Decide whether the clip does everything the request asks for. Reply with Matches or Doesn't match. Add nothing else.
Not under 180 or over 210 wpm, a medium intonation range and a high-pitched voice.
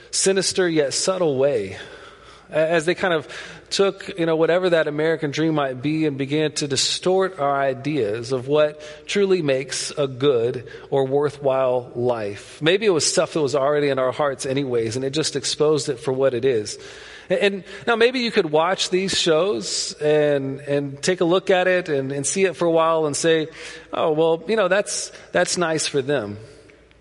Doesn't match